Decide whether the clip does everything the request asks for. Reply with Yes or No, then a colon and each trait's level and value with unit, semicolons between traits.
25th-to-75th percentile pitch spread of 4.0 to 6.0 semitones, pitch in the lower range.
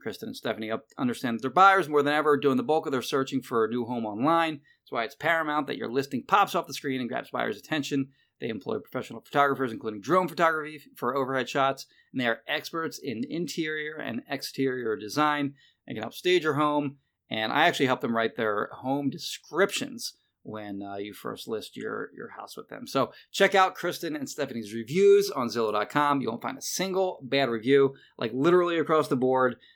No: average, 4.4 semitones; medium, 145 Hz